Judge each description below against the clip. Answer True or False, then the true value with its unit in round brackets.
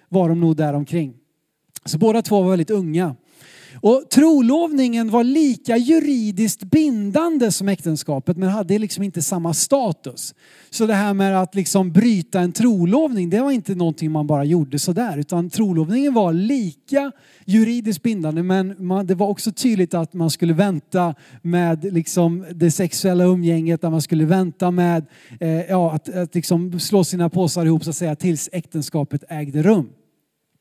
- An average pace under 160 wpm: False (165 wpm)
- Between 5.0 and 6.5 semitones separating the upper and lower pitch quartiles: False (4.4 semitones)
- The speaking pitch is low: False (180 Hz)